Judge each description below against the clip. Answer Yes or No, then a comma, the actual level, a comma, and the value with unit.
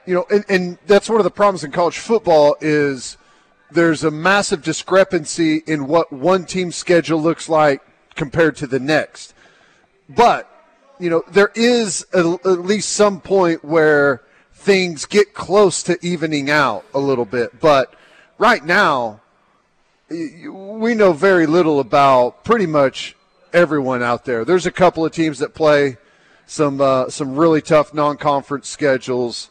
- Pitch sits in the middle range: Yes, medium, 165 Hz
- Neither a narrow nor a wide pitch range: Yes, average, 4.1 semitones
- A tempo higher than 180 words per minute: No, average, 155 wpm